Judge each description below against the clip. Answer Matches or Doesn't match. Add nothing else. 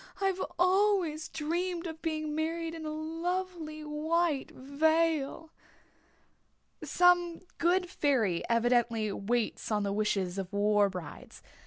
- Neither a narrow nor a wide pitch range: Doesn't match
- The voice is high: Matches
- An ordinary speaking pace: Doesn't match